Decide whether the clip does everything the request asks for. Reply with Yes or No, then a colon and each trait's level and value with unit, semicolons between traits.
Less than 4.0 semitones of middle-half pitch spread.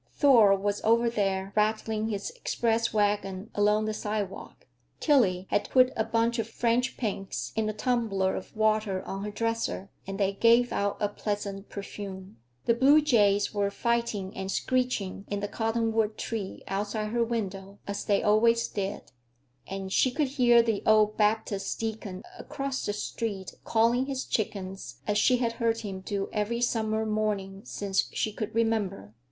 Yes: narrow, 2.5 semitones